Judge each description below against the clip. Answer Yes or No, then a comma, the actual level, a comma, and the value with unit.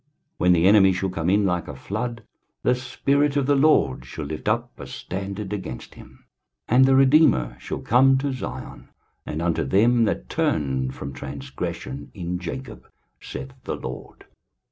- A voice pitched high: No, very low, 95 Hz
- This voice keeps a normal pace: Yes, average, 165 wpm